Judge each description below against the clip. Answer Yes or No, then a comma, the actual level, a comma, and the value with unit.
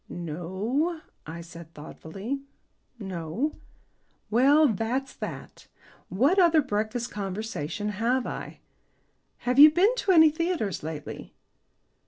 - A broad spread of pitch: Yes, wide, 8.4 semitones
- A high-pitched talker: Yes, high, 225 Hz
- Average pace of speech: No, slow, 105 wpm